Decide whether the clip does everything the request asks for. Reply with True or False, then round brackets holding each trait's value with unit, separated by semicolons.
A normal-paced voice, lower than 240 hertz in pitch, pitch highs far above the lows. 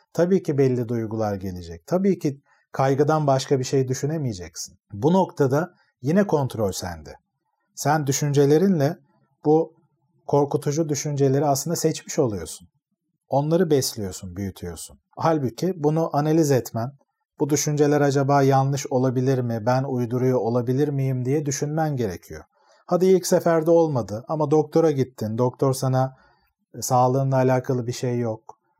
False (125 wpm; 140 Hz; 3.8 semitones)